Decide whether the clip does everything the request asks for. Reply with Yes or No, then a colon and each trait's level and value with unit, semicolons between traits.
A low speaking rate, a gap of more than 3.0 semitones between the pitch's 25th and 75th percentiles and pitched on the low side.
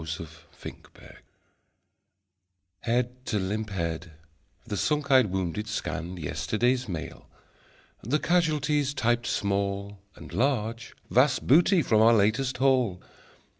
Yes: slow, 115 wpm; average, 4.9 semitones; low, 115 Hz